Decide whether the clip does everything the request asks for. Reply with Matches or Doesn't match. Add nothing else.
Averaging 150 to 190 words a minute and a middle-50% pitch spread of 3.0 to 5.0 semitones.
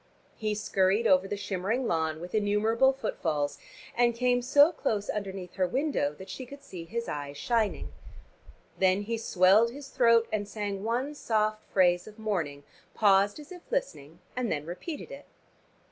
Matches